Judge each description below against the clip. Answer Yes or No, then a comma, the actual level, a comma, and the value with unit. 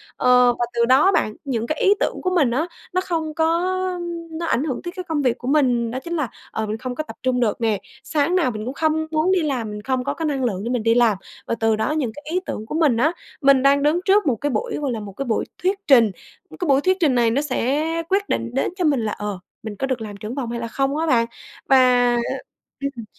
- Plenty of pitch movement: No, average, 4.9 semitones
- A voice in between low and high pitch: No, very high, 265 Hz